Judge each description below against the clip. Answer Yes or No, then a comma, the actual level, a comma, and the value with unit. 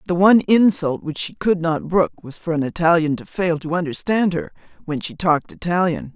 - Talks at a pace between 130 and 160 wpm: No, fast, 205 wpm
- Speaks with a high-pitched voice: No, medium, 170 Hz